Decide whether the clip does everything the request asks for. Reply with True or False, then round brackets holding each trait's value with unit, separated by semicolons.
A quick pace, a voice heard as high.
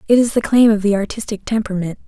True (230 wpm; 210 Hz)